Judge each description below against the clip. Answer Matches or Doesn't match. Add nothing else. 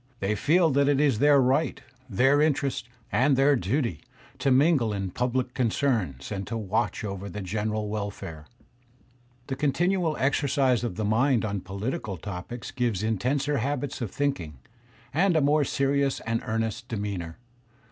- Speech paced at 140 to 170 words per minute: Matches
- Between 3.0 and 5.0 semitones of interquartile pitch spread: Doesn't match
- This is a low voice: Matches